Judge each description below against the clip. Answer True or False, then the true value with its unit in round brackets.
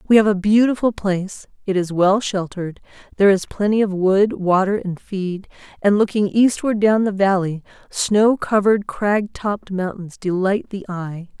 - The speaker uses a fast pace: False (165 wpm)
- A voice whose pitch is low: False (200 Hz)